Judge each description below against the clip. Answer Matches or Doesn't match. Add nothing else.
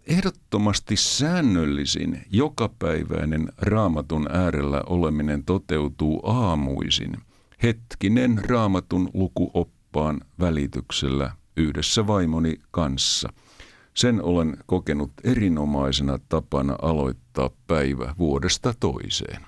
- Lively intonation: Matches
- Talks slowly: Matches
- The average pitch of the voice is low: Matches